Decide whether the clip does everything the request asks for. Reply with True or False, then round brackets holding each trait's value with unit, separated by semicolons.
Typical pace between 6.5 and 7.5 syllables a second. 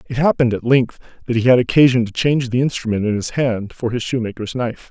True (6.6 syllables/s)